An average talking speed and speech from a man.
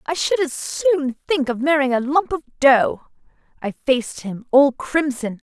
No: average, 175 wpm; female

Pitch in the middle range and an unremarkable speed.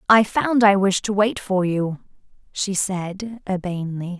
No: high, 195 Hz; average, 155 wpm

